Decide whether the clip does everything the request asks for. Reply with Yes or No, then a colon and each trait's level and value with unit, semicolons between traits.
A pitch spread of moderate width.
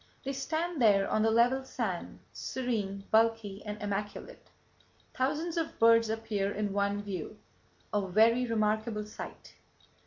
Yes: average, 3.0 semitones